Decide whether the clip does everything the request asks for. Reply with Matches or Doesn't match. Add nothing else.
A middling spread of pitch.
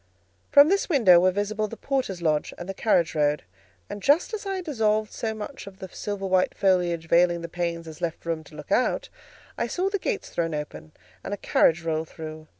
Matches